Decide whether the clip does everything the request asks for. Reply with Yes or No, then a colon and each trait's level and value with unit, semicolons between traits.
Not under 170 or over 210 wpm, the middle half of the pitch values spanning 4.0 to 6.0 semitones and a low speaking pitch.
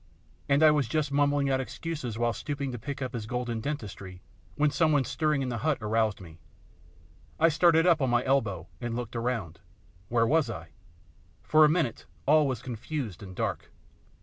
Yes: average, 185 wpm; average, 4.9 semitones; low, 130 Hz